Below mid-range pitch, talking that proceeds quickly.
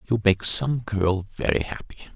No: low, 100 Hz; average, 165 wpm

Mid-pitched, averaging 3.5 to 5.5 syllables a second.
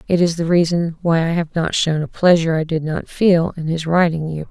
Yes: medium, 165 Hz; 5.4 syllables/s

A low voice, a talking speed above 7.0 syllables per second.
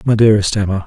Yes: low, 105 Hz; 7.8 syllables/s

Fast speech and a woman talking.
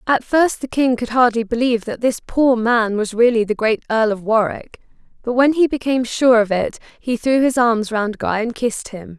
Yes: fast, 220 wpm; female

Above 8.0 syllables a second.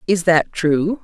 No: 3.5 syllables/s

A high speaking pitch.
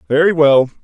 No: medium, 145 Hz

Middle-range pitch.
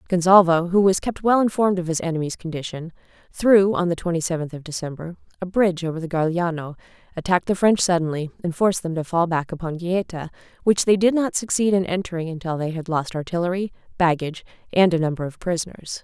Yes: medium, 175 Hz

